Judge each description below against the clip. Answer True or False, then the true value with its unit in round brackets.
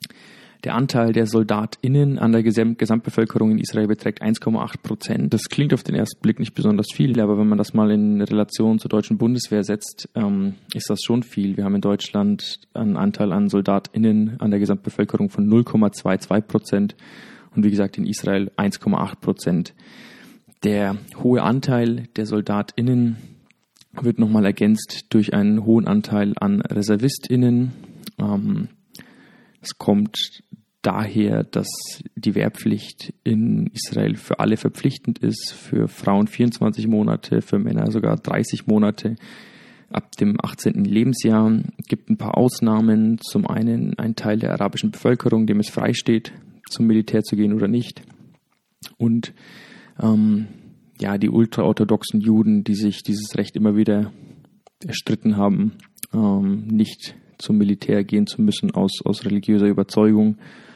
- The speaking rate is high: False (145 wpm)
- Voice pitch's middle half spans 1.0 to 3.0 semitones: False (3.5 semitones)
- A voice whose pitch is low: True (110 Hz)